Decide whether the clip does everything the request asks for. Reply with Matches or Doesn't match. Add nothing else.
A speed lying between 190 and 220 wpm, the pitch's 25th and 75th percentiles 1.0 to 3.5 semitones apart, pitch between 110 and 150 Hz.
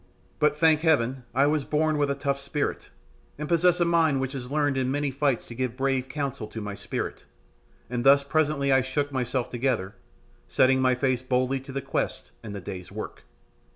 Matches